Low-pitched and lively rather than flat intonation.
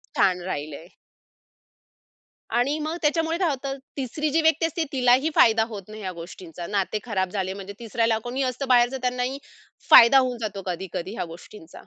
No: high, 235 Hz; wide, 6.1 semitones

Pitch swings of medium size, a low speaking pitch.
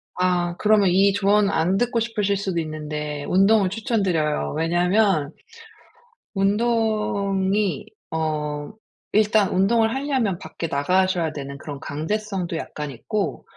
No: average, 4.8 semitones; high, 190 Hz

